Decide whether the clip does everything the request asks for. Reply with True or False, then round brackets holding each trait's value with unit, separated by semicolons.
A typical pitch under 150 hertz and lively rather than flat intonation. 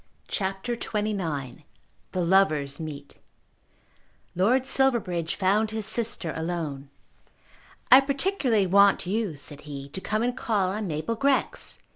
False (195 Hz; 6.1 semitones)